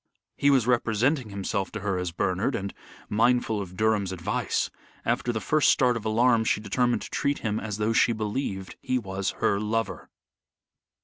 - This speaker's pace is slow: No, average, 175 wpm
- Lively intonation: No, average, 3.4 semitones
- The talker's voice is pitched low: Yes, low, 110 Hz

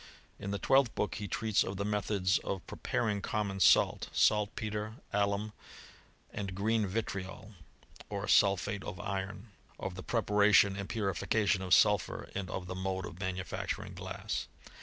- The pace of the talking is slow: No, average, 150 wpm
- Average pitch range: No, narrow, 1.7 semitones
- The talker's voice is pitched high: No, low, 100 Hz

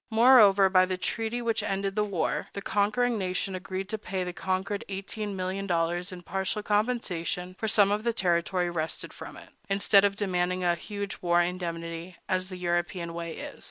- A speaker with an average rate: Yes, average, 185 wpm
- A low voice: No, high, 190 Hz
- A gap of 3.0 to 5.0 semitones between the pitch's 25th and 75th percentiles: No, narrow, 2.5 semitones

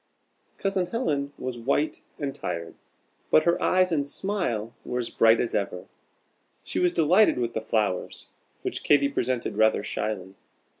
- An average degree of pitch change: No, wide, 7.4 semitones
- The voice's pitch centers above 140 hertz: No, low, 130 Hz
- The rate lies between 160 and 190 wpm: No, average, 150 wpm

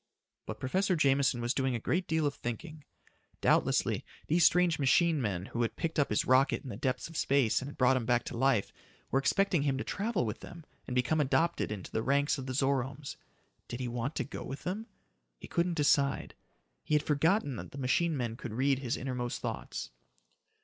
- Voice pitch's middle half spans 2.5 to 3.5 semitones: No, average, 4.0 semitones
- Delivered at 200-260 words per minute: Yes, fast, 205 wpm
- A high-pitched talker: No, low, 135 Hz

